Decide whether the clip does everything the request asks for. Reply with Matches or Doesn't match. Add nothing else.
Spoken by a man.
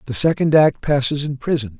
Matches